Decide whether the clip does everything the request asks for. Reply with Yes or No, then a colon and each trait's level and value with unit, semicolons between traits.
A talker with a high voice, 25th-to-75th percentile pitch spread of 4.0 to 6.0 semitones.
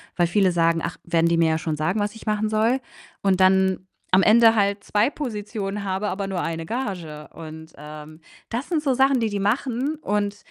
Yes: high, 200 Hz; average, 4.7 semitones